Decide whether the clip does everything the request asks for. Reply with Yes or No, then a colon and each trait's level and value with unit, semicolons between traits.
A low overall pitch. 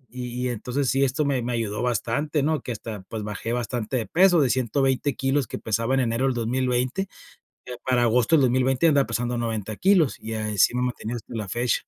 Yes: low, 125 Hz